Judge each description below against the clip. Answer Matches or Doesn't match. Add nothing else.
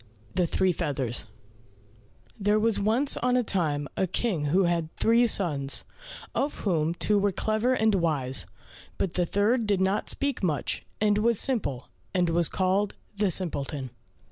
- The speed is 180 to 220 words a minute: Doesn't match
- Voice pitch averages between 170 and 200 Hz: Matches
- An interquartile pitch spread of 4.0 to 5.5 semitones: Matches